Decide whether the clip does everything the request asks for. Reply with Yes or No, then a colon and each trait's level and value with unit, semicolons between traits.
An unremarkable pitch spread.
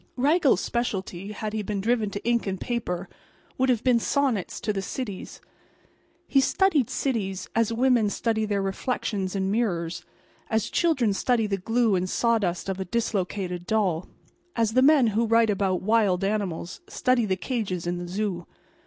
Yes: average, 3.8 semitones